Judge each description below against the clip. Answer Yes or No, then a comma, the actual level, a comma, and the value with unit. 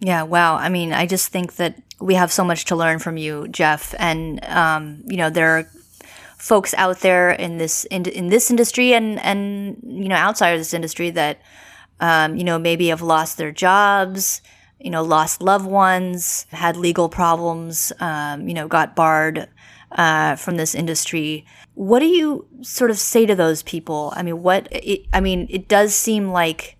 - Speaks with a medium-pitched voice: Yes, medium, 175 Hz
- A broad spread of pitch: No, average, 3.1 semitones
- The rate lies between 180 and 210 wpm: Yes, average, 190 wpm